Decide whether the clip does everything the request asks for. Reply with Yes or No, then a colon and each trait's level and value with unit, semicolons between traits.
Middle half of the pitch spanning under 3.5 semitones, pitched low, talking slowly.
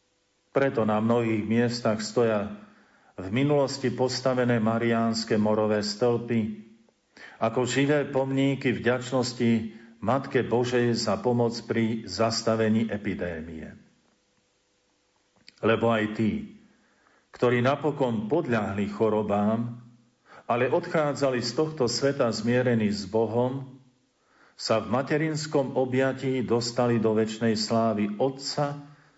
Yes: average, 2.9 semitones; low, 120 Hz; slow, 95 wpm